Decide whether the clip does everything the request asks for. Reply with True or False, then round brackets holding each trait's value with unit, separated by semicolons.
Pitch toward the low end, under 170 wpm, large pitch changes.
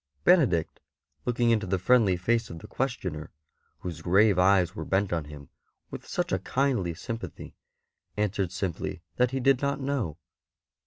True (100 Hz; 155 wpm; 5.8 semitones)